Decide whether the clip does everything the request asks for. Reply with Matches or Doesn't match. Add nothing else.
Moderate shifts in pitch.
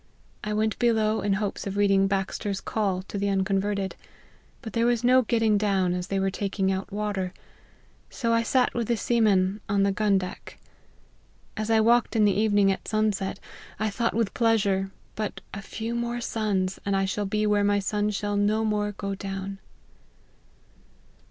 Doesn't match